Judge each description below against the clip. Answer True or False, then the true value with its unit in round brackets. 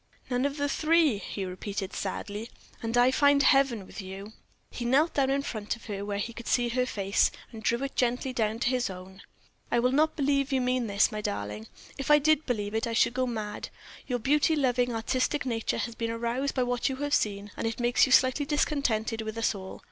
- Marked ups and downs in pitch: False (4.1 semitones)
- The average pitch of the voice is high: True (240 Hz)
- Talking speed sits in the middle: False (225 wpm)